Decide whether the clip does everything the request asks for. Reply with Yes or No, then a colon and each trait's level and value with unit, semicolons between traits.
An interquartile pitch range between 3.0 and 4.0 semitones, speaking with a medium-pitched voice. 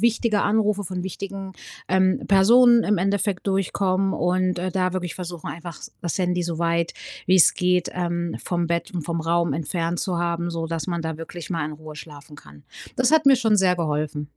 No: narrow, 2.4 semitones; medium, 175 Hz